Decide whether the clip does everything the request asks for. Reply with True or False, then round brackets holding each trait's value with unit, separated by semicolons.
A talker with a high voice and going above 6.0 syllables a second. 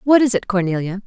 True (210 Hz; 6.3 syllables/s)